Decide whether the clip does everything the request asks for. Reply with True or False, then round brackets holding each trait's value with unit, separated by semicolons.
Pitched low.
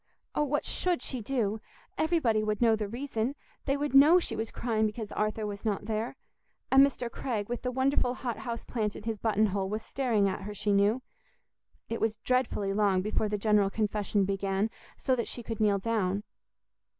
False (220 Hz)